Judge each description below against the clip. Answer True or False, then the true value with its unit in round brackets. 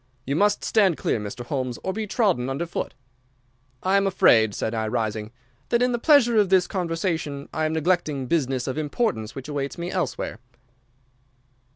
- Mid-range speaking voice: True (160 Hz)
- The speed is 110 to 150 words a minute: False (175 wpm)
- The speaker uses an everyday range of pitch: False (7.1 semitones)